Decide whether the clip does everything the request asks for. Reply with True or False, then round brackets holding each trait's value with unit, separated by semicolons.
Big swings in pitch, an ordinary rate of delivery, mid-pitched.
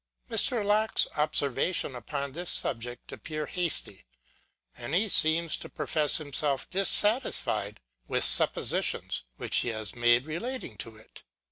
False (6.8 semitones; 125 wpm; 150 Hz)